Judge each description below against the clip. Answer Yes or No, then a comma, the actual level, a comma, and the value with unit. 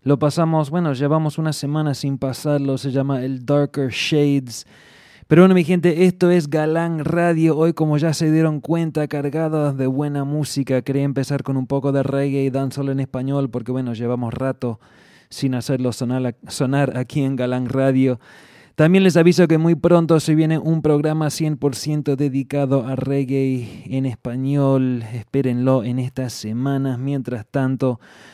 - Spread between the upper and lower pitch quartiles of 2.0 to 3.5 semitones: Yes, average, 2.8 semitones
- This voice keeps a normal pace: Yes, average, 160 wpm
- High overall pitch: No, medium, 140 Hz